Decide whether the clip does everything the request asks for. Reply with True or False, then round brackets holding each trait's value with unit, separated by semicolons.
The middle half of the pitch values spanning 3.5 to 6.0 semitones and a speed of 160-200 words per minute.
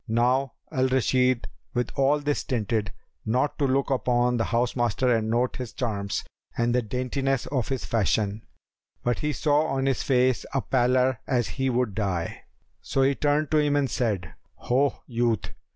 False (2.6 semitones; 170 wpm)